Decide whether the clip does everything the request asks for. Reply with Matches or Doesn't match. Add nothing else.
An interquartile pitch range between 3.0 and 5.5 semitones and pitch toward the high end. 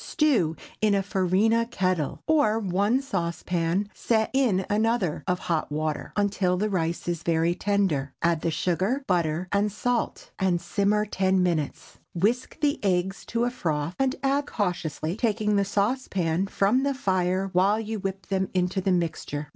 Matches